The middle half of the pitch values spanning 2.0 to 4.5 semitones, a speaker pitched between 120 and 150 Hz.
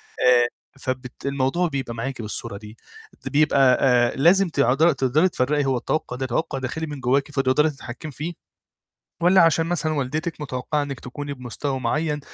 Yes: average, 3.5 semitones; medium, 140 Hz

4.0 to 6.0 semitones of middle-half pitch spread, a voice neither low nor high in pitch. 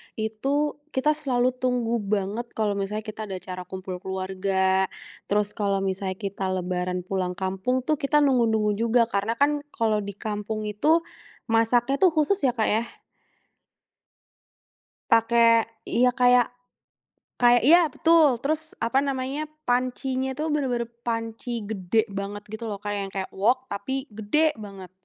No: average, 4.3 semitones; high, 225 Hz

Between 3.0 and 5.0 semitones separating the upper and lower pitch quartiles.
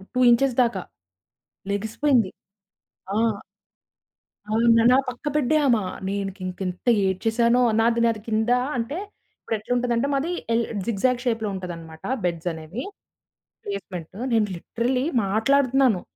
Yes: average, 4.1 semitones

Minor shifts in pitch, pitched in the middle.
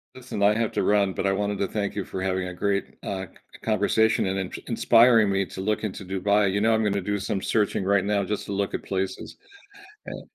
No: narrow, 1.5 semitones; low, 100 Hz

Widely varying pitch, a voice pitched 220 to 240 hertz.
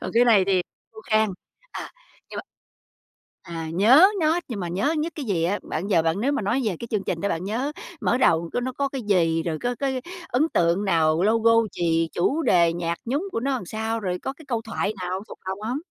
No: wide, 6.1 semitones; high, 210 Hz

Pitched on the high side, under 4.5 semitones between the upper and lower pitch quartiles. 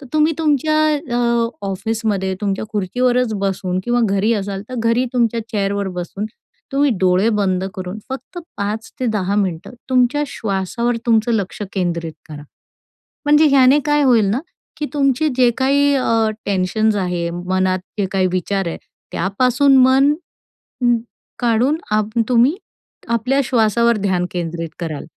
No: high, 220 Hz; average, 5.0 semitones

